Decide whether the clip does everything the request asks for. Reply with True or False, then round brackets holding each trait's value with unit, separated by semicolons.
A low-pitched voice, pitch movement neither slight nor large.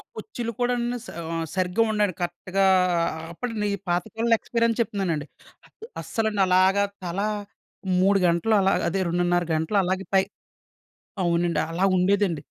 False (195 Hz; 3.7 semitones)